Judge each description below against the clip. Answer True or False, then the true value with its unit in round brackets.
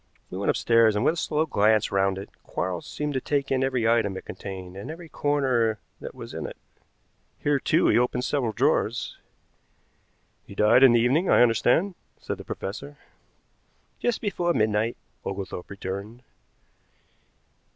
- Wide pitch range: True (5.9 semitones)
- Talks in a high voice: False (120 Hz)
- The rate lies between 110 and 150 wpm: False (160 wpm)